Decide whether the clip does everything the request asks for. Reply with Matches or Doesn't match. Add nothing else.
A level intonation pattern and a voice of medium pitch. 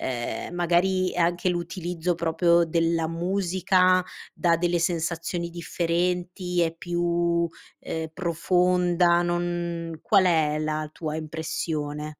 Matches